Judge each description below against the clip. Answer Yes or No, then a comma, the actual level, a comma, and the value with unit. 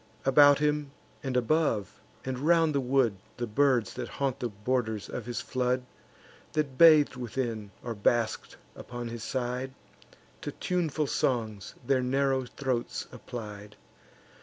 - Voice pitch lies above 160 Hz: No, low, 125 Hz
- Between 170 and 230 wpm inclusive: No, slow, 135 wpm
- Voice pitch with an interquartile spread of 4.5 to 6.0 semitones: No, average, 3.0 semitones